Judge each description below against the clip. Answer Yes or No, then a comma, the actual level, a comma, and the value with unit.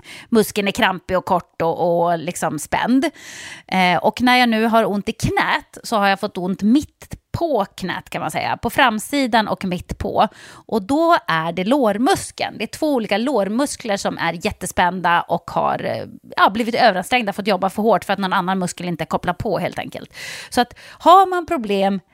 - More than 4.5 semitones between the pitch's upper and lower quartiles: Yes, average, 5.0 semitones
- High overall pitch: Yes, high, 205 Hz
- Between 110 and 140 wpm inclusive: No, average, 190 wpm